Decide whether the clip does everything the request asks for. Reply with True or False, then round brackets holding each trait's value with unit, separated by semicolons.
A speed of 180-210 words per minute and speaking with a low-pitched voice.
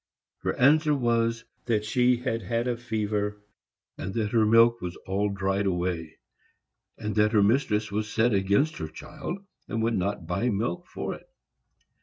False (165 wpm; 110 Hz)